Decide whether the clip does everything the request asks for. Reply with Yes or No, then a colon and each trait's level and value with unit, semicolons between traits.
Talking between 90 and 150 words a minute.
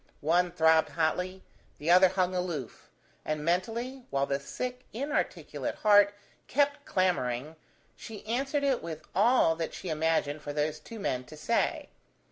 Yes: average, 145 wpm